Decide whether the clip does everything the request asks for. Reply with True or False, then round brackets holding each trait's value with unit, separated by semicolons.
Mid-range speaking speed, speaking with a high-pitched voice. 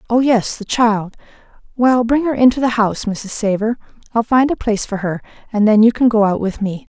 False (225 wpm; 225 Hz)